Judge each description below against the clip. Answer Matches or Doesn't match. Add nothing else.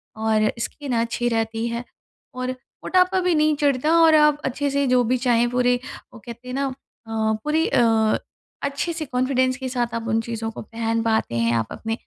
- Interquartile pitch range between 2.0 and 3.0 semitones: Doesn't match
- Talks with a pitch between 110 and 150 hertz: Doesn't match